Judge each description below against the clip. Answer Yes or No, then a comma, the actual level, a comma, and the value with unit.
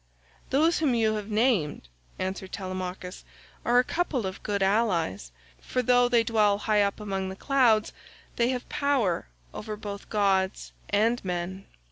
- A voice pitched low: No, high, 210 Hz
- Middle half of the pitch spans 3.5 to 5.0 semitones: Yes, average, 4.1 semitones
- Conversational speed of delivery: Yes, average, 150 wpm